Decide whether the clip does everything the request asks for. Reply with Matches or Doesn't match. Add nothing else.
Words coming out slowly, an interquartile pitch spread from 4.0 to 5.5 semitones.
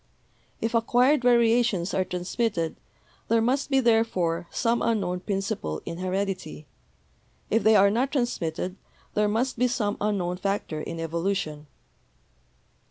Matches